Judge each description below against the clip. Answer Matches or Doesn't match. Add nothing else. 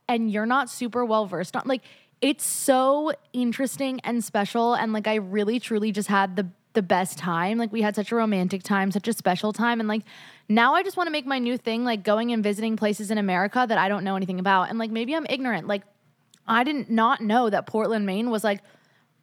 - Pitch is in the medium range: Doesn't match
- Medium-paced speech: Doesn't match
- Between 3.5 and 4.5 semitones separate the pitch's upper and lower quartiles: Doesn't match